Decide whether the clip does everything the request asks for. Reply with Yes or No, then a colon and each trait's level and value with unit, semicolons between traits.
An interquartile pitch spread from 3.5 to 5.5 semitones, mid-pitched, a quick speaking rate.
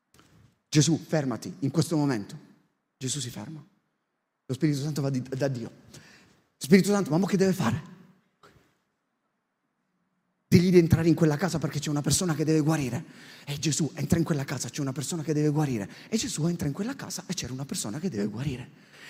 Yes: average, 4.0 semitones; medium, 155 Hz; fast, 185 wpm